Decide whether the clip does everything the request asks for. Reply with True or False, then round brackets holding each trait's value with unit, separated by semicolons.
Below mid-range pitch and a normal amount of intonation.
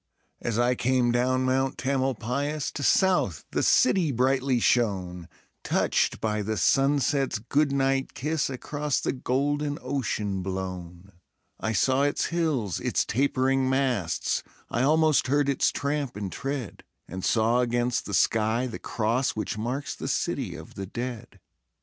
True (130 Hz; 3.9 semitones)